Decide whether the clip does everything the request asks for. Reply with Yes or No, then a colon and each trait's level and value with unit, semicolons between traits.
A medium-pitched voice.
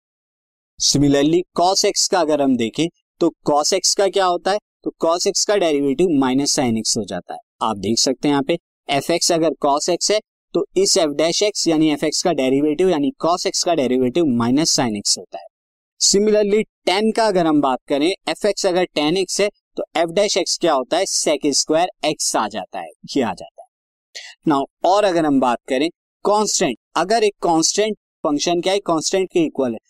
Yes: medium, 175 Hz